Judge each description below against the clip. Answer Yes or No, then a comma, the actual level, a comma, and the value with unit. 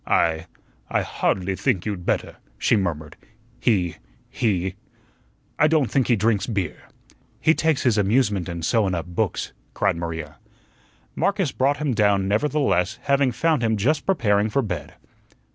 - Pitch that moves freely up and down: Yes, wide, 7.0 semitones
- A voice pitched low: Yes, low, 105 Hz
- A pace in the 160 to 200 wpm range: No, average, 145 wpm